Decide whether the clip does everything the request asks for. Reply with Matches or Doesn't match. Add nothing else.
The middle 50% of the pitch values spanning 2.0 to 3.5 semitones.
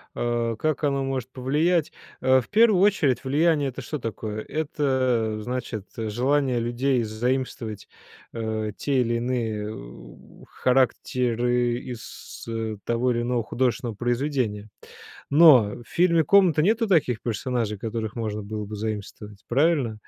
Doesn't match